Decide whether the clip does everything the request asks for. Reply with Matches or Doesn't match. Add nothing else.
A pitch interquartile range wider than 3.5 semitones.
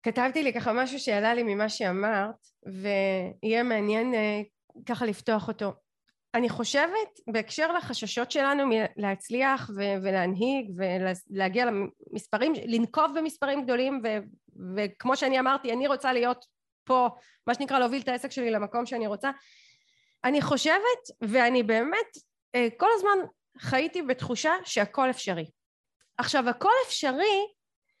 Matches